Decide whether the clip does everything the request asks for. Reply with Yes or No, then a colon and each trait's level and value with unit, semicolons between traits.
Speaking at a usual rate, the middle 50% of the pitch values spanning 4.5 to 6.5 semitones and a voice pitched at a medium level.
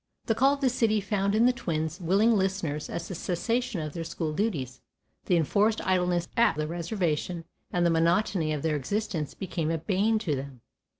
Yes: average, 190 wpm; average, 4.8 semitones; medium, 175 Hz